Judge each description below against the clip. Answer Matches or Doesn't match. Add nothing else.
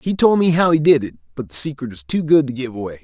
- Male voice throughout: Matches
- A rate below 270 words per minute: Doesn't match